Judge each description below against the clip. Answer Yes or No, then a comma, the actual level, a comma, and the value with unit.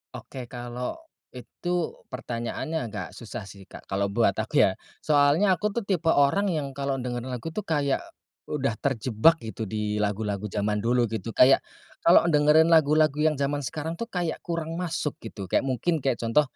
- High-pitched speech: No, medium, 140 Hz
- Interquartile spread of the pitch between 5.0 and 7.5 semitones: Yes, wide, 5.6 semitones